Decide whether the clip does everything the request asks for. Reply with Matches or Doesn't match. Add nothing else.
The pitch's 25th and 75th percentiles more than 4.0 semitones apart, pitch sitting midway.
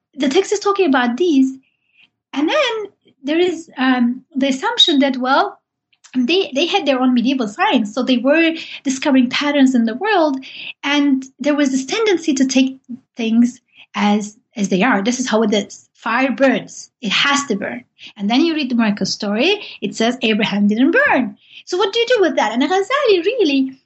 Doesn't match